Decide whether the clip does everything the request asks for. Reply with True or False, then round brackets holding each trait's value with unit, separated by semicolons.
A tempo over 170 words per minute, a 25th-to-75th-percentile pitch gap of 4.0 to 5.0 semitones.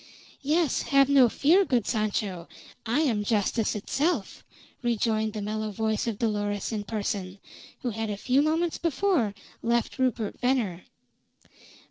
False (135 wpm; 4.7 semitones)